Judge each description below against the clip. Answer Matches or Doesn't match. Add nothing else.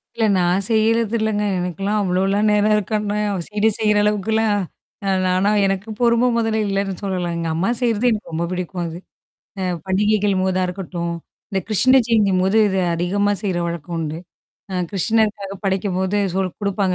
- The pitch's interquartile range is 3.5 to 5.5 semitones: Doesn't match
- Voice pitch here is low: Doesn't match